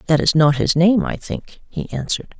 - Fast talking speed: Yes, fast, 225 wpm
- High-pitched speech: No, medium, 170 Hz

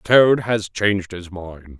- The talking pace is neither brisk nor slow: Yes, average, 165 wpm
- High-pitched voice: No, low, 100 Hz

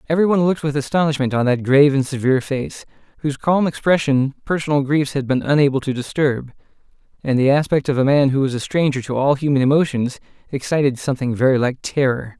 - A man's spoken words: Yes, male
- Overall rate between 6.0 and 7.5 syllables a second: Yes, 6.5 syllables/s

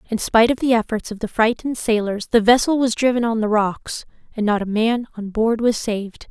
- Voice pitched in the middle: No, high, 225 Hz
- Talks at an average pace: No, fast, 230 wpm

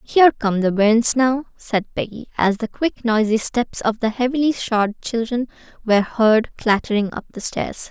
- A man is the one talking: No, female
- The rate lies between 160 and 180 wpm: Yes, average, 175 wpm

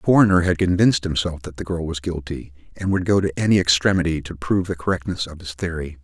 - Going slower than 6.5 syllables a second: No, 6.6 syllables/s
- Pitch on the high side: No, very low, 85 Hz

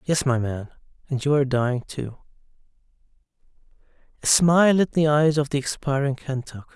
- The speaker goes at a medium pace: Yes, average, 150 wpm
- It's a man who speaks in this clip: Yes, male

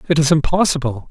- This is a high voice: No, medium, 150 Hz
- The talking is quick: No, average, 165 wpm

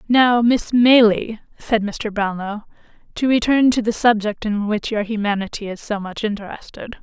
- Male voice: No, female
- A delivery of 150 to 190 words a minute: Yes, average, 160 wpm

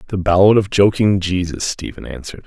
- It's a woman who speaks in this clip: No, male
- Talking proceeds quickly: No, average, 170 wpm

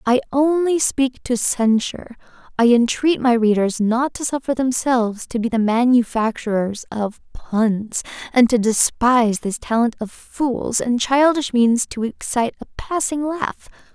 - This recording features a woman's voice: Yes, female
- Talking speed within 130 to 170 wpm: Yes, average, 145 wpm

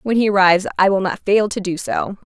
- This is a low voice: No, high, 190 Hz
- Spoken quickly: Yes, fast, 260 wpm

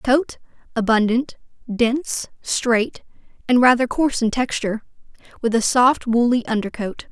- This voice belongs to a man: No, female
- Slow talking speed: Yes, slow, 110 wpm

